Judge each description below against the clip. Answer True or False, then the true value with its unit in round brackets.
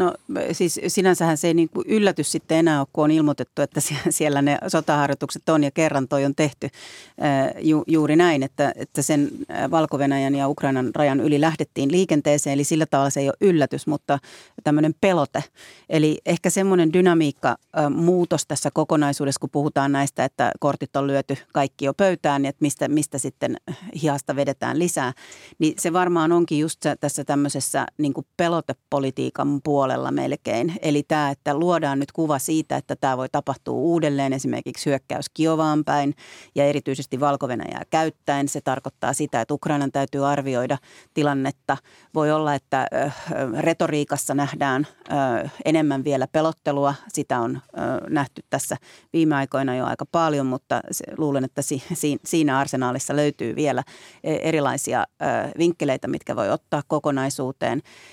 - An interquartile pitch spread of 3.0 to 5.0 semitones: False (2.4 semitones)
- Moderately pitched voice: True (145 Hz)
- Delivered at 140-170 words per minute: True (145 wpm)